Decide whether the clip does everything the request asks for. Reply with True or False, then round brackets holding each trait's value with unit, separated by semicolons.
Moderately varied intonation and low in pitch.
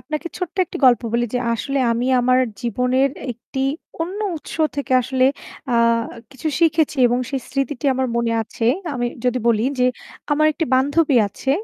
False (3.3 semitones; 260 Hz)